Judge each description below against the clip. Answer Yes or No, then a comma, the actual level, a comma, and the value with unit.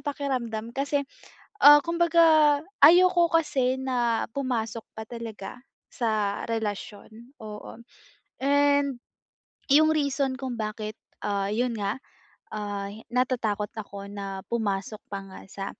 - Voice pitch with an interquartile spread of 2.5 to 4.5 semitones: No, average, 5.1 semitones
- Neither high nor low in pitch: No, high, 235 Hz